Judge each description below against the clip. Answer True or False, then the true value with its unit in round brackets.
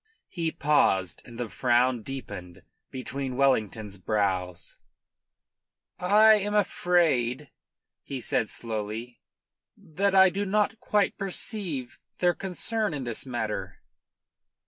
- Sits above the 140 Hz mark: False (135 Hz)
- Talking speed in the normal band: False (105 wpm)